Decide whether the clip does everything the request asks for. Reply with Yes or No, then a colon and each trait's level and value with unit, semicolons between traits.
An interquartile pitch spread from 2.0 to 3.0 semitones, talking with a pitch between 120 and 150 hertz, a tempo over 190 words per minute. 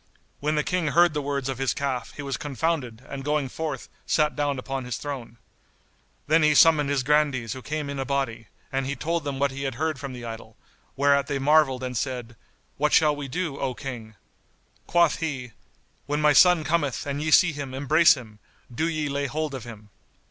Yes: average, 2.7 semitones; medium, 140 Hz; fast, 205 wpm